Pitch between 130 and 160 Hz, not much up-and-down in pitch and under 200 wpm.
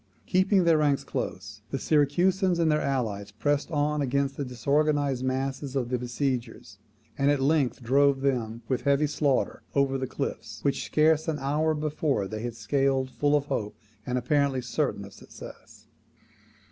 No: medium, 140 Hz; average, 3.0 semitones; average, 160 wpm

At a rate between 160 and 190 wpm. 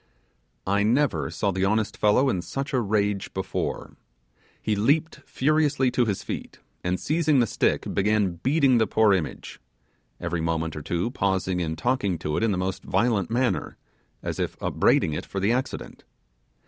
Yes: average, 170 wpm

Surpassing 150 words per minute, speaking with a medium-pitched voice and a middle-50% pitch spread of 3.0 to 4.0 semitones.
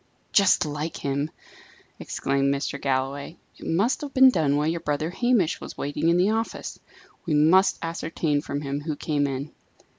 Yes: average, 170 wpm; medium, 155 Hz; average, 3.7 semitones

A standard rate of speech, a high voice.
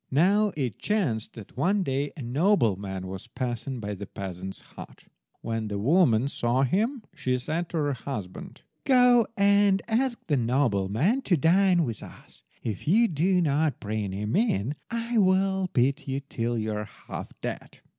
No: average, 165 wpm; medium, 140 Hz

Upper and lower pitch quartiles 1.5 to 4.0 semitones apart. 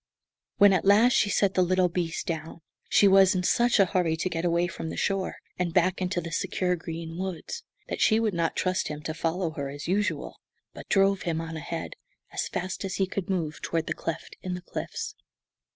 Yes: average, 2.7 semitones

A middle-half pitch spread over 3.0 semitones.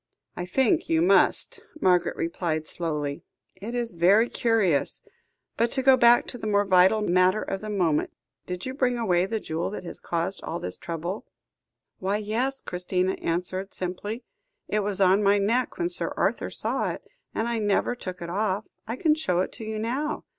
Yes: average, 4.2 semitones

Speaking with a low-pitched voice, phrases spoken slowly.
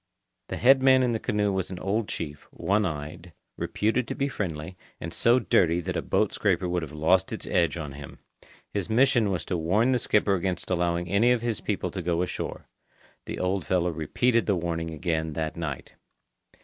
No: very low, 90 Hz; average, 200 wpm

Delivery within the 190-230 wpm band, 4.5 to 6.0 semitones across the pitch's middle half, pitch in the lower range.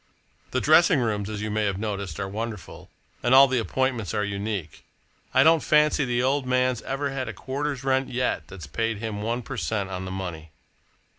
Yes: average, 200 wpm; average, 4.8 semitones; low, 115 Hz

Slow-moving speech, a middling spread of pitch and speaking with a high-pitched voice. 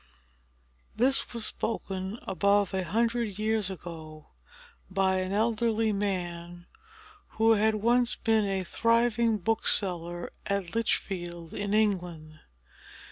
Yes: slow, 105 wpm; average, 3.8 semitones; high, 200 Hz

